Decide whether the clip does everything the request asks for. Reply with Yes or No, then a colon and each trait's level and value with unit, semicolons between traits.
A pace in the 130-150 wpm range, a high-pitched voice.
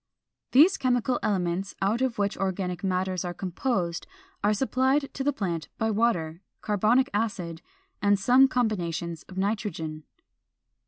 Yes: average, 140 wpm; high, 200 Hz